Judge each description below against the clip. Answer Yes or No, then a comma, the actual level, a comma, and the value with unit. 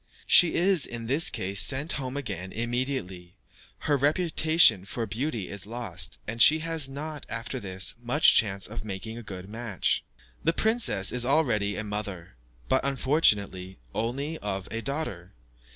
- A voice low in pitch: Yes, low, 115 Hz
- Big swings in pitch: Yes, wide, 6.2 semitones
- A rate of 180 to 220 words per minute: No, average, 150 wpm